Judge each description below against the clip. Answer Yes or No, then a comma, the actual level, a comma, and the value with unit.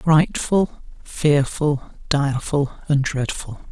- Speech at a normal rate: No, slow, 80 wpm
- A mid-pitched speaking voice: Yes, medium, 145 Hz